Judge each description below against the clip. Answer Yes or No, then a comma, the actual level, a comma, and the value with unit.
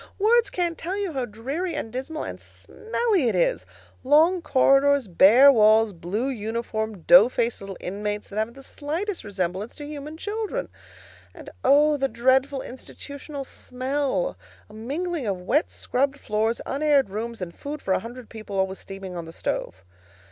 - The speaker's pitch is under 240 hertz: No, very high, 260 Hz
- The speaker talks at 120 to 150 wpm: No, average, 160 wpm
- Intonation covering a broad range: Yes, wide, 6.0 semitones